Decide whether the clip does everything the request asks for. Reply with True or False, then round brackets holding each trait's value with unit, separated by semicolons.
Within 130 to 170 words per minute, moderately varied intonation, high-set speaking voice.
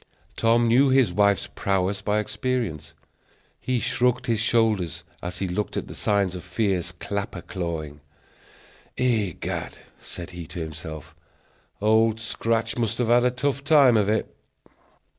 False (140 wpm; 4.6 semitones; 105 Hz)